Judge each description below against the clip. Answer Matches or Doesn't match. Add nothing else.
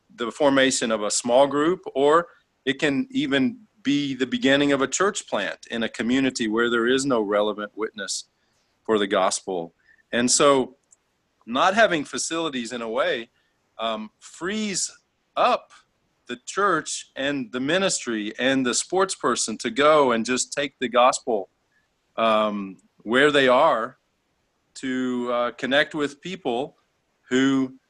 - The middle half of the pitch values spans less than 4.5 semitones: Matches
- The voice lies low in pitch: Matches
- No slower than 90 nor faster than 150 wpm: Matches